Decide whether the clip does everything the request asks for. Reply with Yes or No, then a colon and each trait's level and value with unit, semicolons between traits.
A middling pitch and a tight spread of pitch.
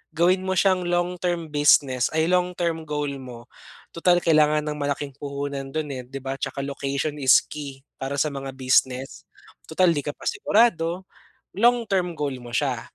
No: medium, 150 Hz; average, 4.2 semitones